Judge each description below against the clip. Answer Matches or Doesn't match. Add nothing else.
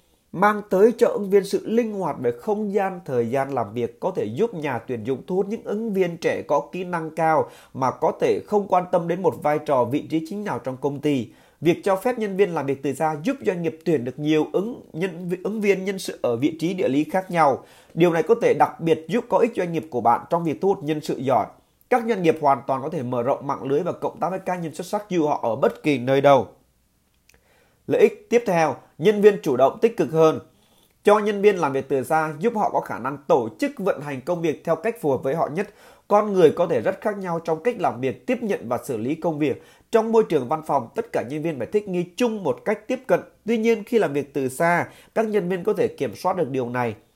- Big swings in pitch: Matches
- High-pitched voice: Doesn't match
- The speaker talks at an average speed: Doesn't match